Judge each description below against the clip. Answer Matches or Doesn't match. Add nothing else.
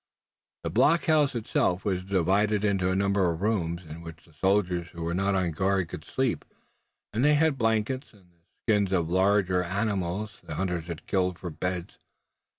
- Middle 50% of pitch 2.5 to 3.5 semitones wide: Matches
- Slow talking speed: Doesn't match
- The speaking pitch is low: Matches